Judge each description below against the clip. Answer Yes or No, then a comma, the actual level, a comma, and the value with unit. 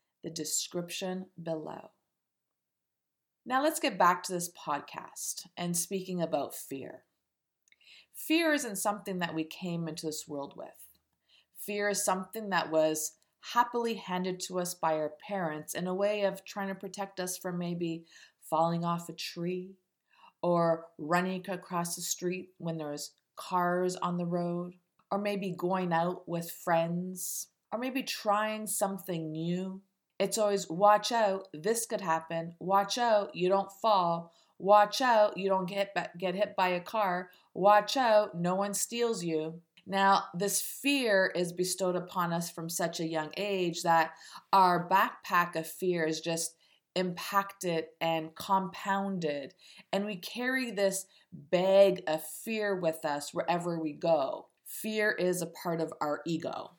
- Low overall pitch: No, medium, 180 Hz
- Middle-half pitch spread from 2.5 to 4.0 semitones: Yes, average, 3.0 semitones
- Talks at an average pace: Yes, average, 150 wpm